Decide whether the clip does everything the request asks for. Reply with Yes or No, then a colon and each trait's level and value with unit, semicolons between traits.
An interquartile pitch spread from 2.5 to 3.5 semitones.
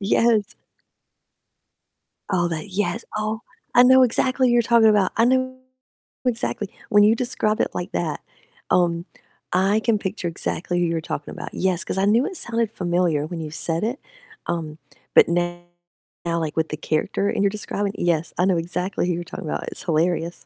No: average, 4.6 semitones